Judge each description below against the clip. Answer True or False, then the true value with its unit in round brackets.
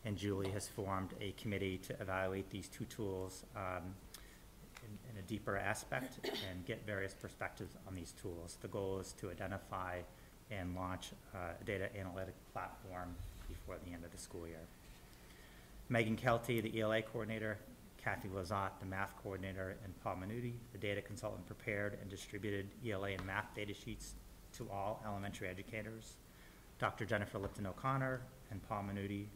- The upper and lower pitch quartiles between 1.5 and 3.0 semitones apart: True (2.4 semitones)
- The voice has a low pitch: True (100 Hz)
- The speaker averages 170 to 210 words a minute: False (160 wpm)